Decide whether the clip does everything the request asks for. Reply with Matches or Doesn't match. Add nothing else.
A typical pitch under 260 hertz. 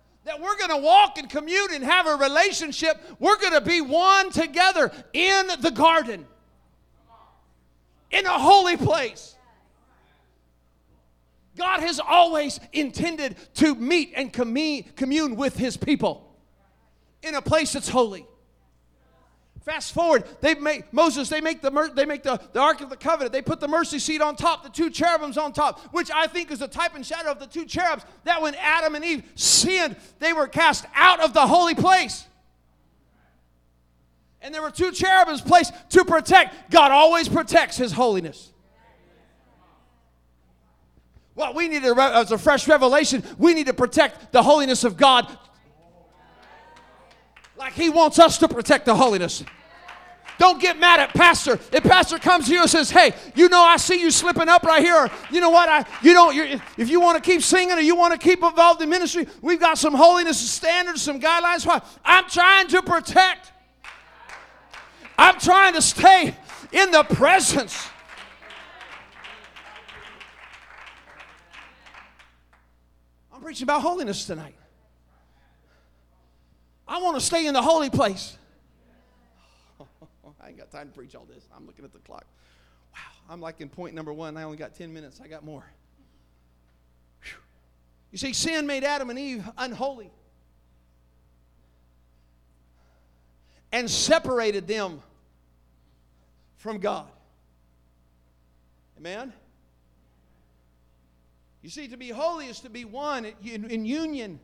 Doesn't match